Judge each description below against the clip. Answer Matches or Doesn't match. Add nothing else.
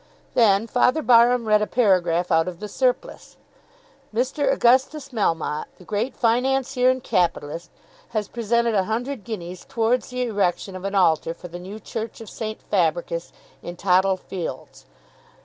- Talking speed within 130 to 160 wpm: Matches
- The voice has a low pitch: Doesn't match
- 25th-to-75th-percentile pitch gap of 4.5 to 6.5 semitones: Matches